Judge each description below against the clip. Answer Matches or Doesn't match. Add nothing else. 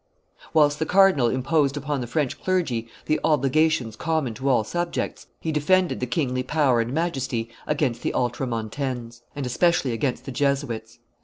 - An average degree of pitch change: Matches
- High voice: Doesn't match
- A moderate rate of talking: Matches